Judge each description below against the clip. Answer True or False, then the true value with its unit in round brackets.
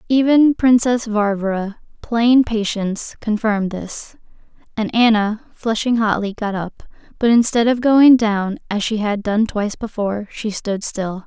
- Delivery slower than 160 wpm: True (145 wpm)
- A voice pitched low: False (220 Hz)